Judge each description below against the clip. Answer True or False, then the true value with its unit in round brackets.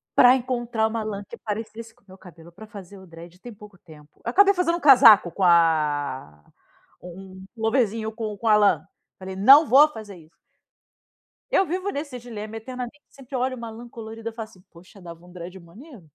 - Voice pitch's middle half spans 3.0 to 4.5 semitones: False (5.2 semitones)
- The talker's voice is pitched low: False (215 Hz)